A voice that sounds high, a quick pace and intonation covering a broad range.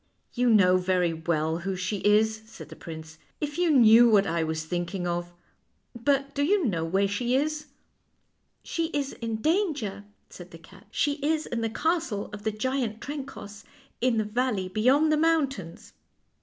No: high, 220 Hz; average, 185 wpm; wide, 7.3 semitones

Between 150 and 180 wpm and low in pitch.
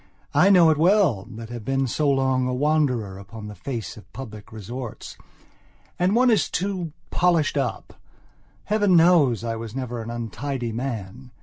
Yes: average, 170 wpm; low, 130 Hz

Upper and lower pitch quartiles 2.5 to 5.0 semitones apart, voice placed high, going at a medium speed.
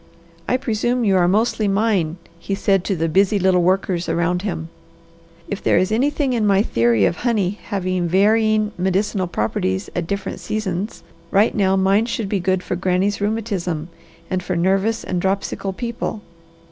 Yes: average, 3.1 semitones; high, 195 Hz; average, 165 wpm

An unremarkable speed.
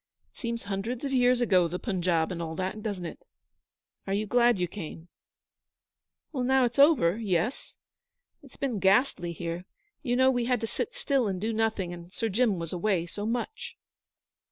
Yes: average, 185 wpm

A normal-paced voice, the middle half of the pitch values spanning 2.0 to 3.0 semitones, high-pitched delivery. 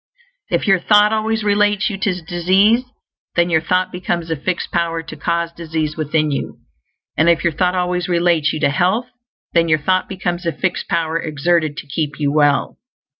No: average, 185 wpm; average, 2.7 semitones; medium, 170 Hz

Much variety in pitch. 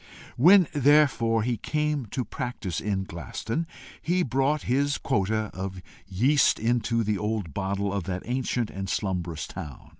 Yes: wide, 5.9 semitones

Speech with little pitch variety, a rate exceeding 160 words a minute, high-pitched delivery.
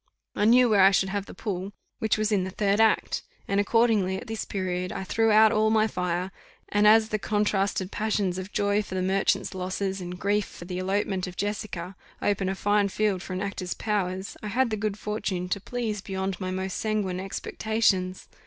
Yes: narrow, 2.3 semitones; fast, 205 wpm; high, 200 Hz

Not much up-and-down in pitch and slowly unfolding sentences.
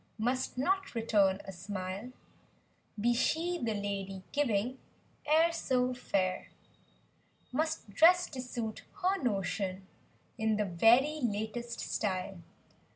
No: average, 5.0 semitones; slow, 110 wpm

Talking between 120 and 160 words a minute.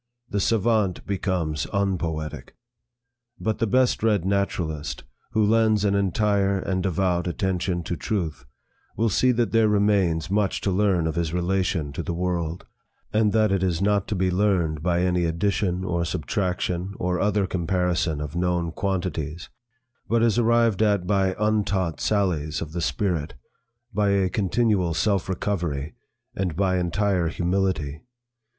Yes: average, 145 wpm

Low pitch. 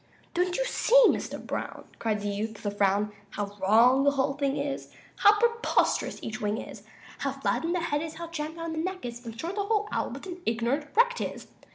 No: very high, 285 Hz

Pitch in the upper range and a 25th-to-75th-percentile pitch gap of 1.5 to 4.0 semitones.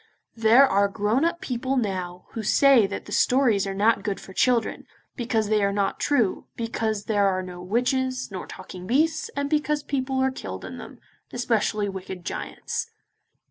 No: high, 225 Hz; average, 4.7 semitones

